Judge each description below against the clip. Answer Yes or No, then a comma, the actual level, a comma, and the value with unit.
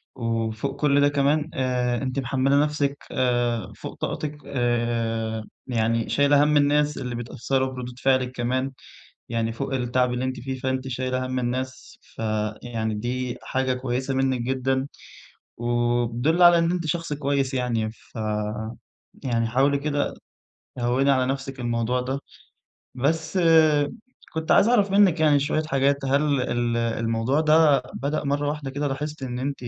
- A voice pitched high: No, low, 130 Hz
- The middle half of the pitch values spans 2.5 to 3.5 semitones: Yes, average, 2.8 semitones